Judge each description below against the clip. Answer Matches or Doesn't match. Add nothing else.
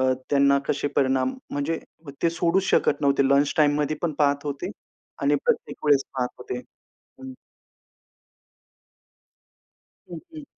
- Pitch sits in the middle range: Matches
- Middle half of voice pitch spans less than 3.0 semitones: Matches